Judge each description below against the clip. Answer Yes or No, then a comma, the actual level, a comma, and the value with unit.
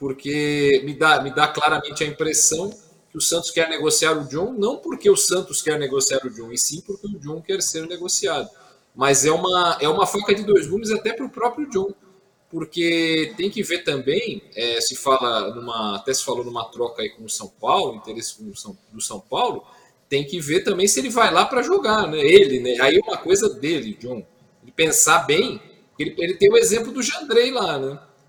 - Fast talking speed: Yes, fast, 215 wpm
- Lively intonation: Yes, wide, 6.7 semitones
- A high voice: No, medium, 160 Hz